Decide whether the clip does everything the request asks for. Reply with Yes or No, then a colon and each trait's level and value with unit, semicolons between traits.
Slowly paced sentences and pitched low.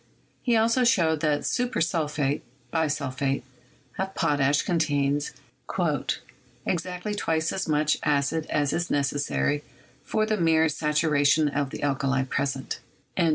No: slow, 120 wpm; medium, 150 Hz